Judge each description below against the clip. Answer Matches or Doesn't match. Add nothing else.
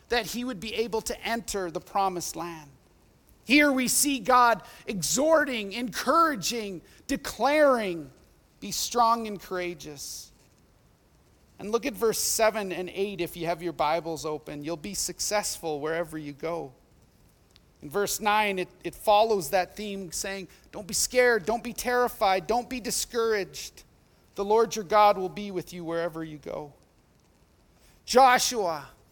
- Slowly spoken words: Doesn't match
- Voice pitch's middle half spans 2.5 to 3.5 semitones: Doesn't match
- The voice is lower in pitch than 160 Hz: Doesn't match